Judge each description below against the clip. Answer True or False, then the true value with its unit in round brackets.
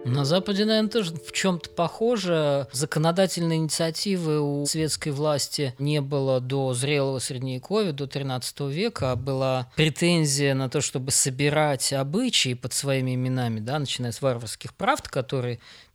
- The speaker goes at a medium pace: True (140 wpm)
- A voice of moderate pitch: True (145 Hz)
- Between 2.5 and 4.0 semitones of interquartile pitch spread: True (3.6 semitones)